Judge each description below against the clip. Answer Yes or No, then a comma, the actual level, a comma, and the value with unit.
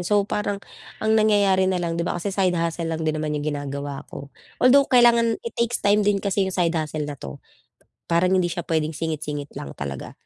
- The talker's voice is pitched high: No, medium, 175 Hz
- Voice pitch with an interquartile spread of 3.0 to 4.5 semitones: No, average, 5.0 semitones